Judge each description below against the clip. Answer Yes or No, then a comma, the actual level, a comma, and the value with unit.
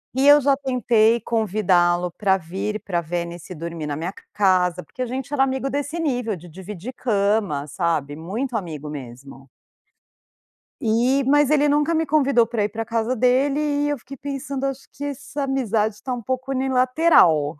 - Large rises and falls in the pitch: Yes, wide, 7.2 semitones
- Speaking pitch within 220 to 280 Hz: Yes, high, 230 Hz